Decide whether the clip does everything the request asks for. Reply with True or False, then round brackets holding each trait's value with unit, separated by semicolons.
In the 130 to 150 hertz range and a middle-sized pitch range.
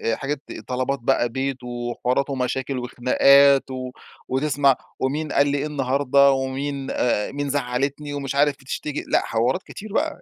False (135 Hz; 1.9 semitones)